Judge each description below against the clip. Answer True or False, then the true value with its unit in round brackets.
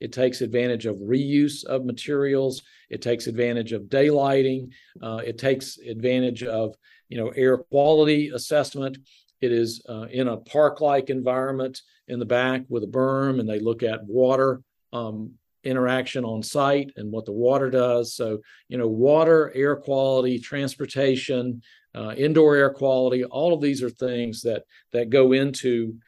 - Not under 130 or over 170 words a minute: True (160 wpm)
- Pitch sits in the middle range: False (130 Hz)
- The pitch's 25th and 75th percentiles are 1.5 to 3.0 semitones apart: True (2.4 semitones)